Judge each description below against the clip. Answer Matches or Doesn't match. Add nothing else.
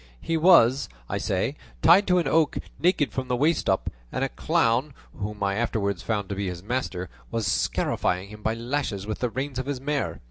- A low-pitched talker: Matches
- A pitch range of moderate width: Doesn't match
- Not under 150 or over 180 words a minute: Doesn't match